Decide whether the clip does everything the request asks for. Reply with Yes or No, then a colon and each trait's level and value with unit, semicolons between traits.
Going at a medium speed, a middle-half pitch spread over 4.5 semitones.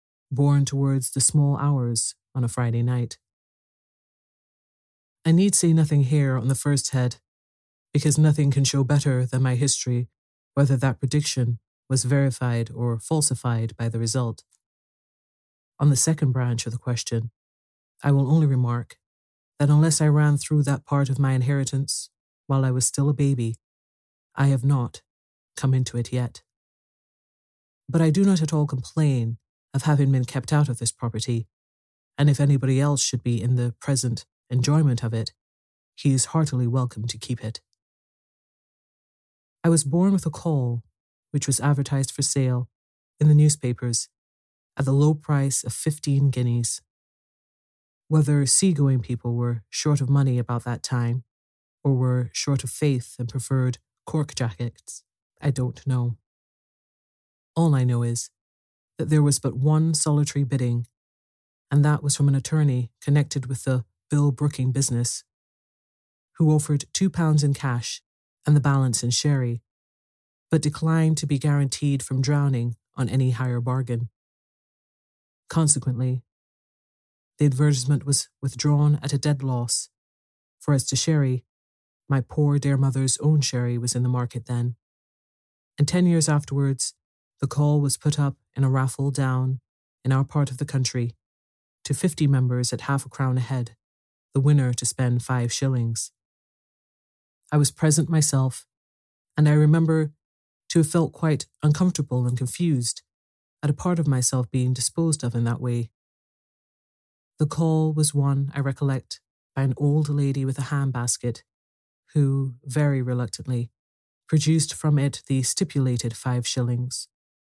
No: average, 150 wpm; average, 3.4 semitones